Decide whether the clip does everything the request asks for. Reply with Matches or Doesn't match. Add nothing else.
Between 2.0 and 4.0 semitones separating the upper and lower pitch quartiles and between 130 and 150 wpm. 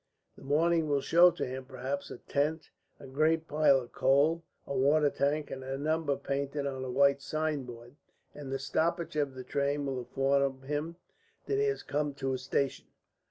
Doesn't match